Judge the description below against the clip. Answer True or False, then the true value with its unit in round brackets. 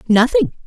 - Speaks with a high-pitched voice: True (280 Hz)